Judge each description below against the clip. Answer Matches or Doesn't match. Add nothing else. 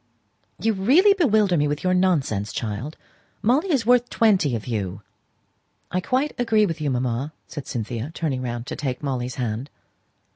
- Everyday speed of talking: Matches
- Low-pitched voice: Doesn't match